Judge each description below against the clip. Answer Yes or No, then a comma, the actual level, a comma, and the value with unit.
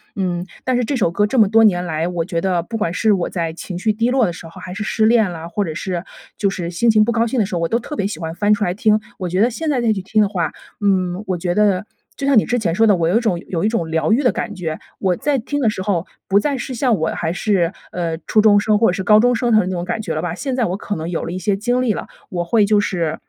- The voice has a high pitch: Yes, high, 200 Hz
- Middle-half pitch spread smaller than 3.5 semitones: No, average, 4.3 semitones